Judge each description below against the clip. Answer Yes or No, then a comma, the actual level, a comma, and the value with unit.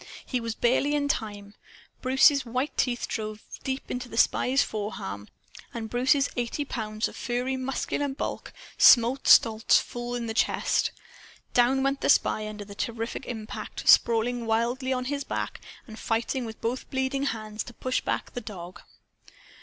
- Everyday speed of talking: Yes, average, 160 wpm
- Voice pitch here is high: Yes, high, 240 Hz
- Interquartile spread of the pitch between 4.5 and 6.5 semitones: No, average, 3.0 semitones